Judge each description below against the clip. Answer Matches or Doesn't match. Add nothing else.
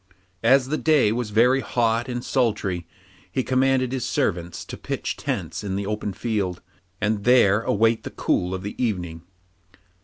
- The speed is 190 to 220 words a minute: Doesn't match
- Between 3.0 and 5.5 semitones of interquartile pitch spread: Matches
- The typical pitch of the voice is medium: Doesn't match